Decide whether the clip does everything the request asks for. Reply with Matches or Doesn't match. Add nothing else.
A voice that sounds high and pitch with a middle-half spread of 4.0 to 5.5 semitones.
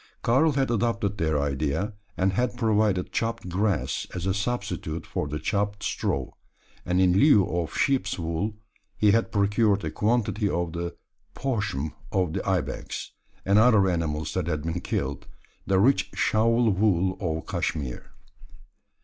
Doesn't match